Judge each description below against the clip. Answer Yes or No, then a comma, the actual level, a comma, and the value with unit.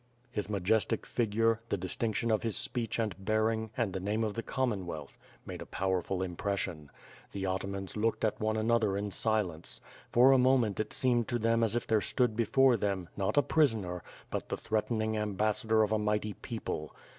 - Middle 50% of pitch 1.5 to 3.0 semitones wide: Yes, average, 2.7 semitones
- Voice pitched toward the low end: Yes, low, 110 Hz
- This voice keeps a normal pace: Yes, average, 190 wpm